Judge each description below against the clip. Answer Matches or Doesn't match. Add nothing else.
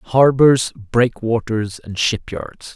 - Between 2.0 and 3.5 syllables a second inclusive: Matches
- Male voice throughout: Matches